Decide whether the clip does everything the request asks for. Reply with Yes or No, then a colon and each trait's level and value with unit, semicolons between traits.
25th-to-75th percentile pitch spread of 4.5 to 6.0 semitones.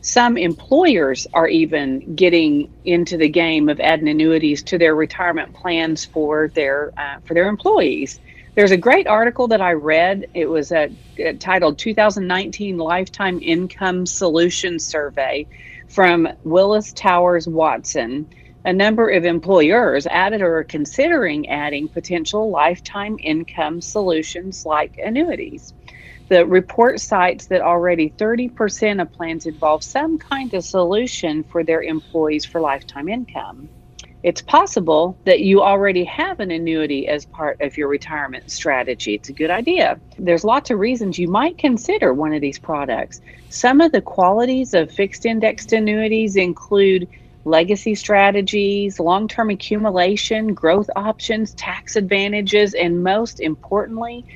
Yes: average, 4.8 semitones